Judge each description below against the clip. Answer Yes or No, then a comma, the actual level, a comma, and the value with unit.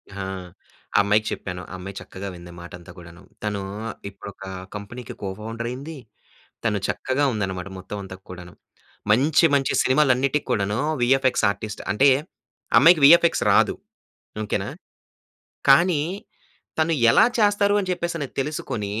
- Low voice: Yes, low, 115 Hz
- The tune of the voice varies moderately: No, wide, 6.4 semitones